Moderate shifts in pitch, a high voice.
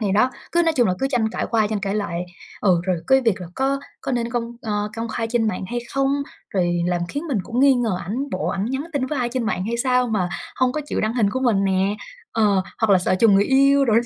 Yes: average, 4.6 semitones; high, 230 Hz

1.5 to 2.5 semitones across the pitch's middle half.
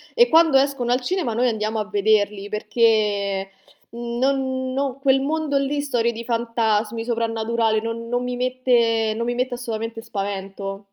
No: average, 2.9 semitones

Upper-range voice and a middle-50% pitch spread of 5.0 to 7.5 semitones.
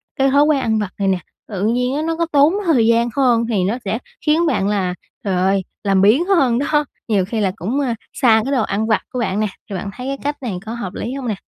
Yes: high, 235 Hz; average, 5.3 semitones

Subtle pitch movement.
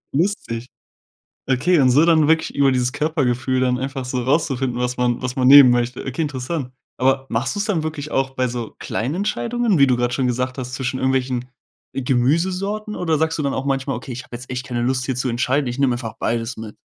No: average, 3.1 semitones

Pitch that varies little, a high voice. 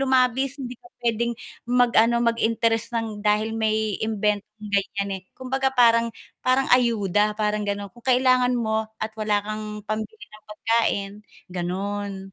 Yes: narrow, 2.3 semitones; high, 220 Hz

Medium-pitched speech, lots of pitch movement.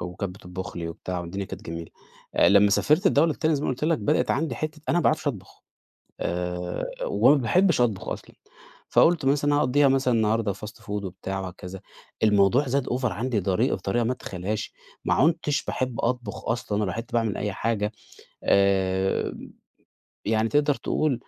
No: low, 115 Hz; wide, 6.5 semitones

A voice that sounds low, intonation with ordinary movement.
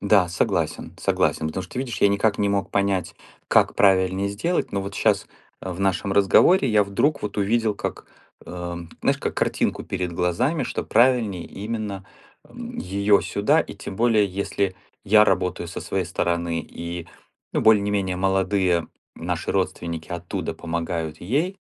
Yes: low, 100 Hz; average, 3.0 semitones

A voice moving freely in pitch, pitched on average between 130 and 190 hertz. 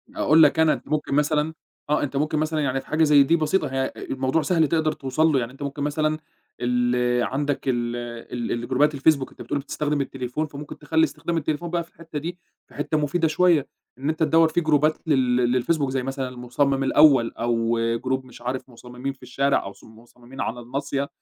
No: average, 3.5 semitones; medium, 140 Hz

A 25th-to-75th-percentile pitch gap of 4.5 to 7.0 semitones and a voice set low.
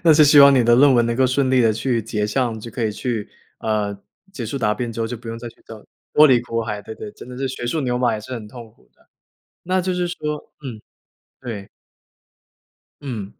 No: average, 3.2 semitones; low, 120 Hz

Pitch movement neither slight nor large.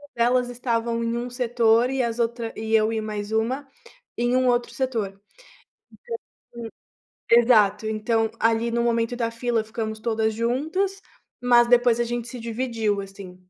No: narrow, 1.6 semitones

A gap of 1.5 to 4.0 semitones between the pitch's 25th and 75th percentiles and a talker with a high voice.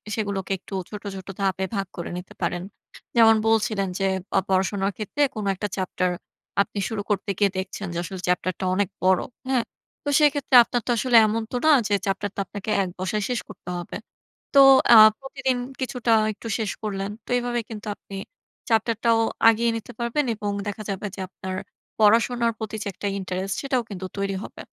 Yes: average, 3.2 semitones; high, 205 Hz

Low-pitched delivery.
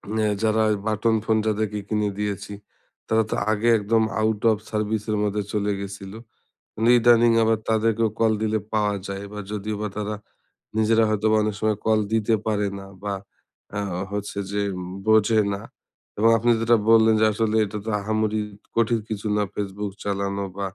Yes: low, 110 Hz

